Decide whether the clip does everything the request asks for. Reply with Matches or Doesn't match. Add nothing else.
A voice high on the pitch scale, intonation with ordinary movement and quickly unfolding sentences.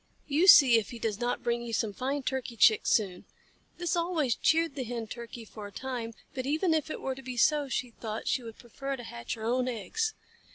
Matches